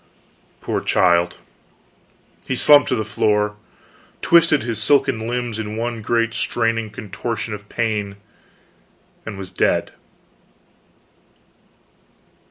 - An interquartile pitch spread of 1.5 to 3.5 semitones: Yes, narrow, 2.4 semitones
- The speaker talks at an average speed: No, slow, 100 wpm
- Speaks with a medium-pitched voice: No, low, 110 Hz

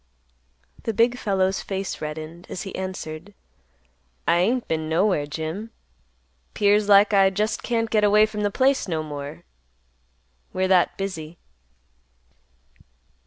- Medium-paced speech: No, slow, 125 wpm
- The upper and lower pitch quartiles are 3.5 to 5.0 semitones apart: Yes, average, 4.5 semitones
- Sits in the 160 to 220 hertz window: Yes, high, 190 Hz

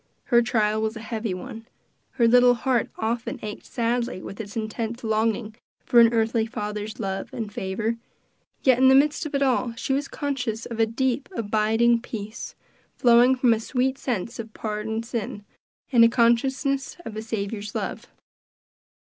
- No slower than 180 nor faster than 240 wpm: No, average, 165 wpm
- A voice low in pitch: No, high, 230 Hz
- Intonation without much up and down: Yes, narrow, 2.2 semitones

